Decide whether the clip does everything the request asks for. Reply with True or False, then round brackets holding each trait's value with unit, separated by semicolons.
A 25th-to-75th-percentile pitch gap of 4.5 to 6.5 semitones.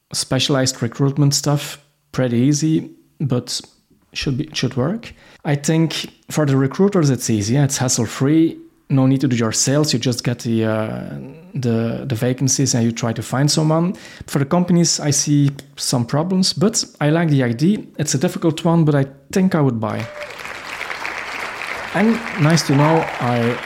False (4.1 semitones)